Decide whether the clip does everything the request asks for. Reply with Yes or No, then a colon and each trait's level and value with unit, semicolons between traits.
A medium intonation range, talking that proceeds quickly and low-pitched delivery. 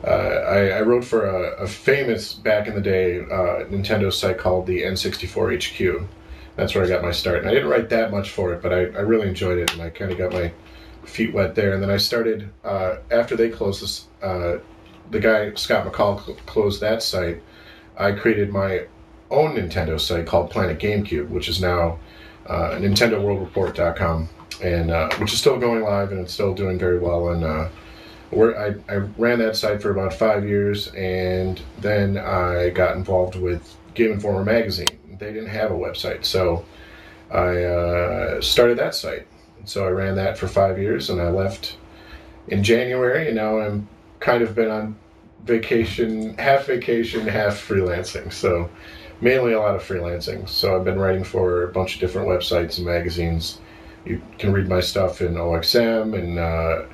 Yes: average, 3.6 semitones; fast, 185 wpm; very low, 95 Hz